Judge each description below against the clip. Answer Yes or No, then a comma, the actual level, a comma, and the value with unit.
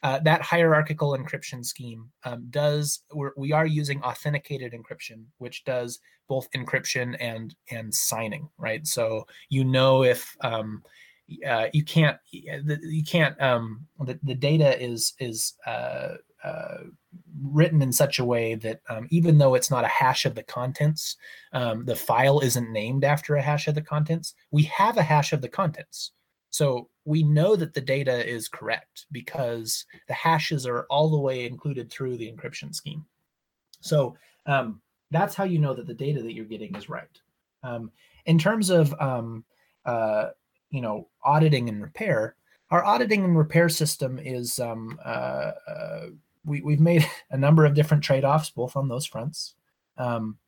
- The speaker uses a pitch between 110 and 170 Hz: Yes, medium, 140 Hz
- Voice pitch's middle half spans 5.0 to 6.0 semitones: No, average, 4.0 semitones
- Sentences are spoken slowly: No, average, 165 wpm